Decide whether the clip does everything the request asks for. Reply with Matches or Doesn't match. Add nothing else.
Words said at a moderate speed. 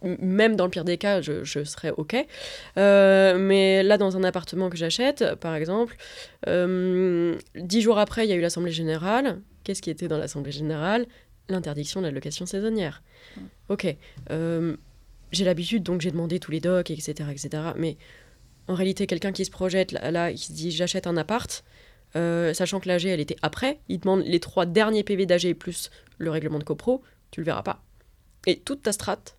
Matches